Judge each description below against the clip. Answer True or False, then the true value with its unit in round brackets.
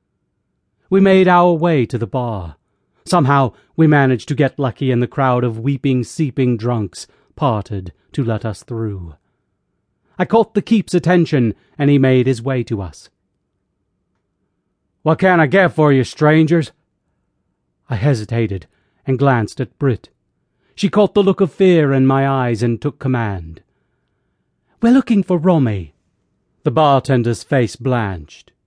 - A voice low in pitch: True (130 Hz)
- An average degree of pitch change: False (6.1 semitones)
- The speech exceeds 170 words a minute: False (145 wpm)